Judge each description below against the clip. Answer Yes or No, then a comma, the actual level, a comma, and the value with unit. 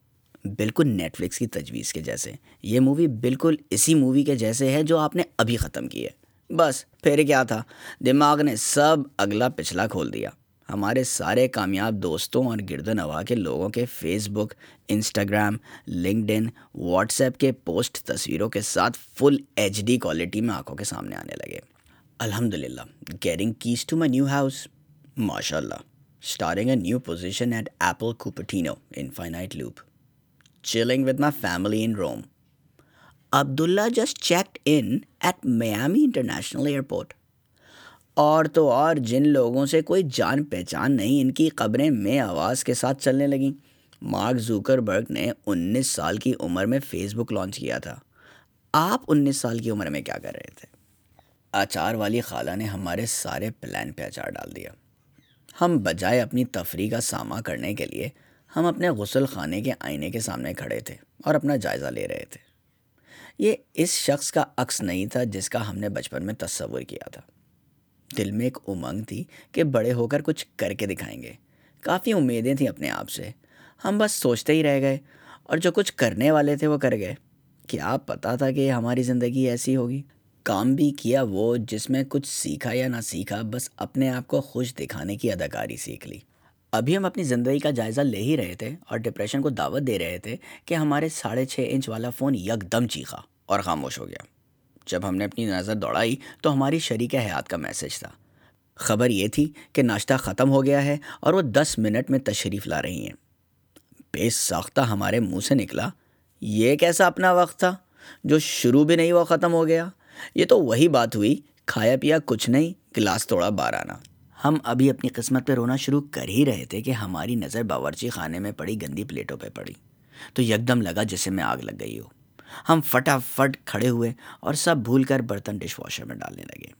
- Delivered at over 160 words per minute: Yes, average, 185 wpm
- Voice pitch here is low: Yes, low, 125 Hz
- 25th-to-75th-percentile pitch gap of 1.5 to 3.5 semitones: No, average, 4.9 semitones